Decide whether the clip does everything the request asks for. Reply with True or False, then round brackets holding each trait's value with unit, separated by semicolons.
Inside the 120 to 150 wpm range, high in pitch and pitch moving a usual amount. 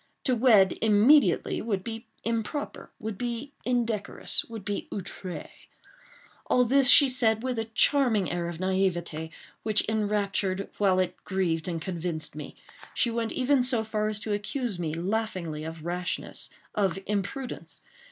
True (135 wpm; 210 Hz; 4.0 semitones)